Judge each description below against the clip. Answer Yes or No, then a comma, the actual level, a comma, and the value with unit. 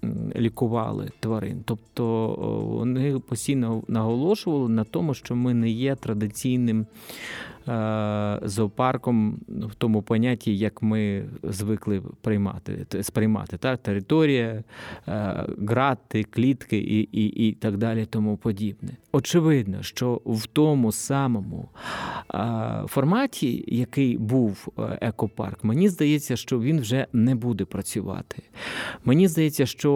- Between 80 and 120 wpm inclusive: Yes, slow, 105 wpm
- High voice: No, low, 115 Hz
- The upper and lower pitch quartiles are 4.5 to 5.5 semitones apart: No, average, 3.7 semitones